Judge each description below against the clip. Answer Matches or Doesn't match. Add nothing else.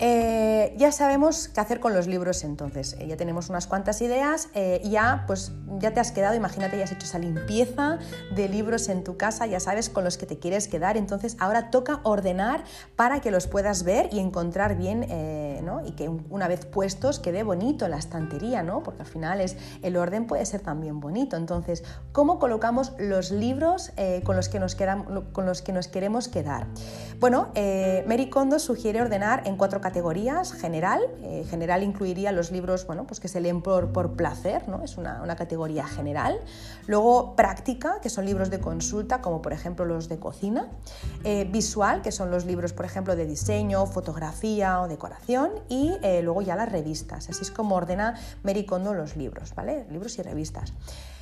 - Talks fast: Matches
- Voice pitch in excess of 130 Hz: Matches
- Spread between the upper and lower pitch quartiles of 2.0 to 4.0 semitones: Doesn't match